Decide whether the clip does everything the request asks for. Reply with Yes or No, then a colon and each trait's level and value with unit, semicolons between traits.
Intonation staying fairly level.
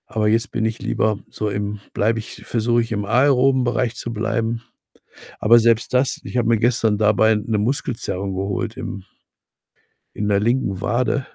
Yes: narrow, 2.2 semitones